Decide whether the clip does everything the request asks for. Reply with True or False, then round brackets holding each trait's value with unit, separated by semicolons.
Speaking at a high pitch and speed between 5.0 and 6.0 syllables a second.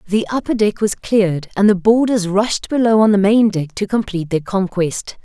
True (205 Hz; 5.1 syllables/s)